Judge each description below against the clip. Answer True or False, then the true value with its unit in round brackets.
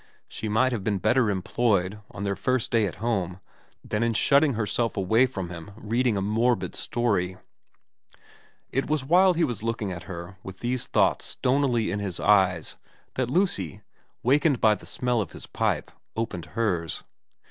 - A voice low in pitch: True (110 Hz)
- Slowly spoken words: False (180 wpm)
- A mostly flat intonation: False (4.6 semitones)